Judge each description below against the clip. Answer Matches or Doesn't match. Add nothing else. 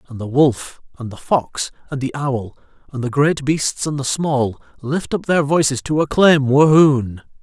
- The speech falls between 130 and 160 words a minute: Doesn't match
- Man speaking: Matches